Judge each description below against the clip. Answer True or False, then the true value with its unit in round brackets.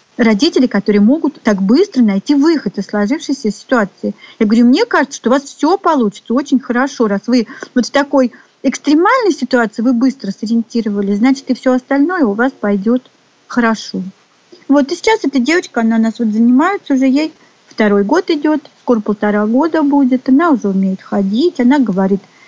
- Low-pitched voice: False (255 Hz)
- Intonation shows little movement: False (4.6 semitones)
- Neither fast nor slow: False (170 wpm)